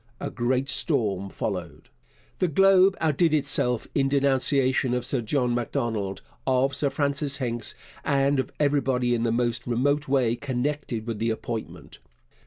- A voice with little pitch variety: No, average, 3.0 semitones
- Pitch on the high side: No, low, 130 Hz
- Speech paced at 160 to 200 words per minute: No, average, 145 wpm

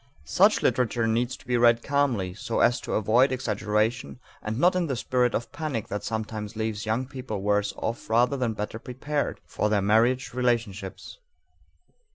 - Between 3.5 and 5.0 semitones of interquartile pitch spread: No, average, 3.1 semitones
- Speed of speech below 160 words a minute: No, average, 170 wpm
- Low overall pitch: Yes, low, 115 Hz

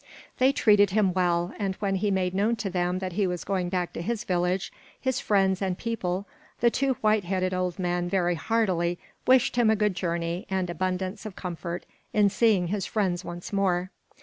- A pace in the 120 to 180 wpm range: No, average, 195 wpm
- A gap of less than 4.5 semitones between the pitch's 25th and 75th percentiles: Yes, average, 2.7 semitones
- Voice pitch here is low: No, high, 190 Hz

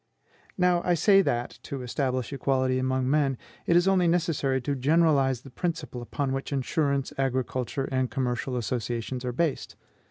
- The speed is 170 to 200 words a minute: No, average, 155 wpm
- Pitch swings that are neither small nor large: Yes, average, 3.5 semitones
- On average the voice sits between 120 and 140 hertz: Yes, low, 135 Hz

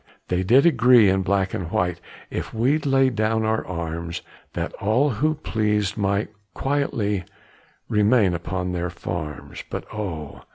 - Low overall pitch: Yes, low, 105 Hz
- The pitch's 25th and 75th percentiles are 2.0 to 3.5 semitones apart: No, average, 4.9 semitones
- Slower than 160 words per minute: Yes, average, 140 wpm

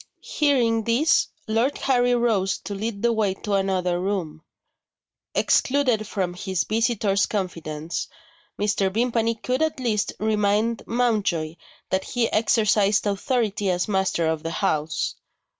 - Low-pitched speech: No, high, 210 Hz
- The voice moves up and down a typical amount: Yes, average, 3.5 semitones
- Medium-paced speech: No, slow, 125 wpm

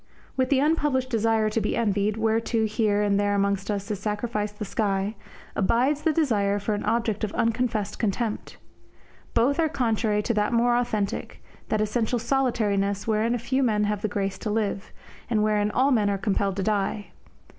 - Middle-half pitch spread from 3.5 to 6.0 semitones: No, narrow, 2.6 semitones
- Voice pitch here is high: Yes, high, 215 Hz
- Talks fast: No, average, 180 wpm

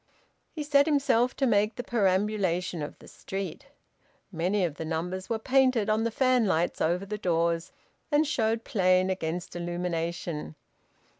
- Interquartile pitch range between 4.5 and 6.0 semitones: Yes, average, 5.1 semitones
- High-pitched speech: Yes, high, 195 Hz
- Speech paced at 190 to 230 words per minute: No, average, 145 wpm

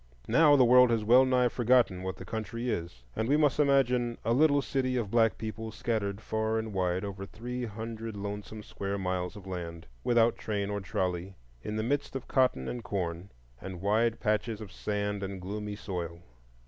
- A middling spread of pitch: Yes, average, 3.7 semitones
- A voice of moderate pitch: No, low, 110 Hz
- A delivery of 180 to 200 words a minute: Yes, average, 185 wpm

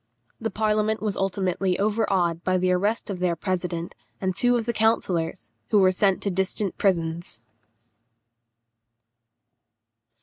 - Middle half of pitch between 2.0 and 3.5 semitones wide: Yes, average, 2.9 semitones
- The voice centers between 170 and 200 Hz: Yes, high, 190 Hz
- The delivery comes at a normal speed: No, slow, 130 wpm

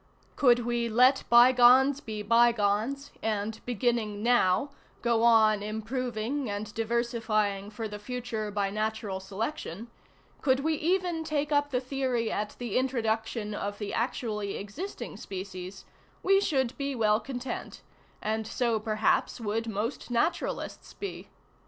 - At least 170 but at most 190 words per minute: No, slow, 135 wpm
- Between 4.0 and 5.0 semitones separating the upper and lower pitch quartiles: No, average, 3.2 semitones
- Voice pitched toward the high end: Yes, high, 230 Hz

